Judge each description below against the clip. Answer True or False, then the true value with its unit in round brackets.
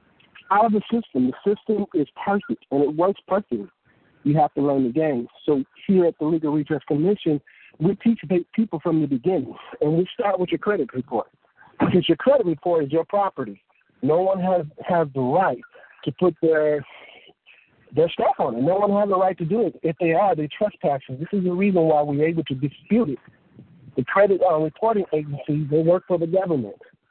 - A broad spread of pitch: False (4.8 semitones)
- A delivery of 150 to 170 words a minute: False (195 wpm)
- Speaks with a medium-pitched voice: True (170 Hz)